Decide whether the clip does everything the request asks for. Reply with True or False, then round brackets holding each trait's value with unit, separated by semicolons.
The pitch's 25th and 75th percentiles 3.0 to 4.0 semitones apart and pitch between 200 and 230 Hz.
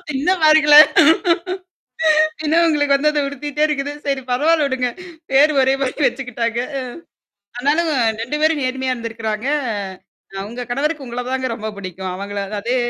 False (3.7 semitones; 265 Hz)